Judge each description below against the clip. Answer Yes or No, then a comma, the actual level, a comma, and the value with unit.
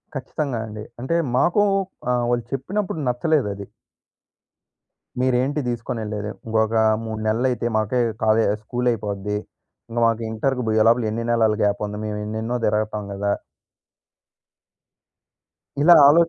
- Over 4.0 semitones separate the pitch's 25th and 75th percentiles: No, average, 2.8 semitones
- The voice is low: Yes, low, 115 Hz